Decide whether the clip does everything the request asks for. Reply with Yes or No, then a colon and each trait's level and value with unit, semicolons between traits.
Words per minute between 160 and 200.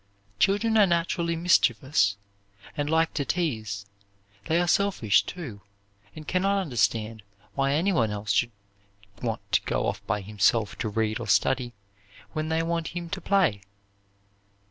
No: average, 145 wpm